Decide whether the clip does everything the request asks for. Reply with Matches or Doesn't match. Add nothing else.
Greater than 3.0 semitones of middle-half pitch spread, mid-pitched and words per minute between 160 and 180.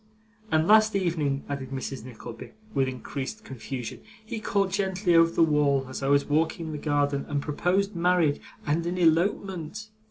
Matches